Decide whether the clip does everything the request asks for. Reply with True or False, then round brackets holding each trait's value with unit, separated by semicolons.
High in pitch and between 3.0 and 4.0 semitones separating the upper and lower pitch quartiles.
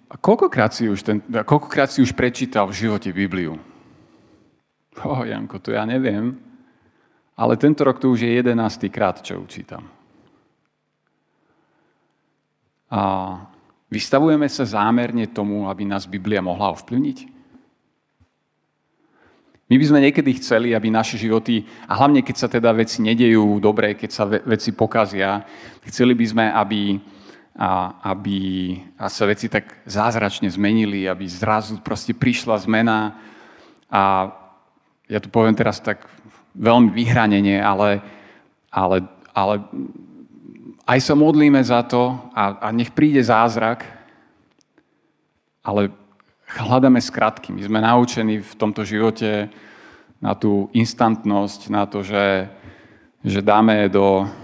False (110 Hz; 3.3 semitones)